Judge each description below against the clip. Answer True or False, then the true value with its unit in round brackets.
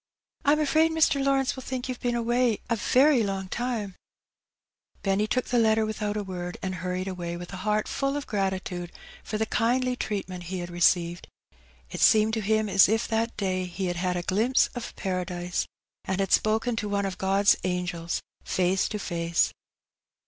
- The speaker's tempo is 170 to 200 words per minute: True (185 wpm)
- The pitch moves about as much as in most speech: True (4.3 semitones)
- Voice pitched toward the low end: False (200 Hz)